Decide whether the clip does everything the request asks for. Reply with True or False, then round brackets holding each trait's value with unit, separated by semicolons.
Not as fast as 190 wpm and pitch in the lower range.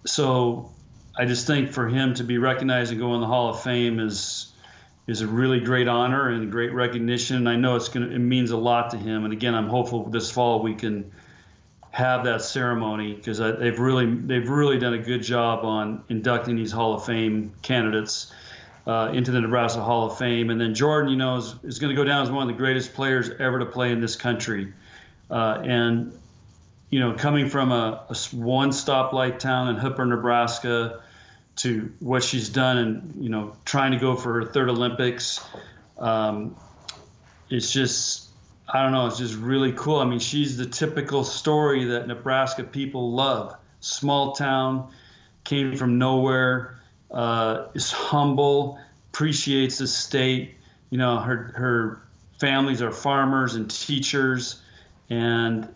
True (175 wpm; 120 Hz)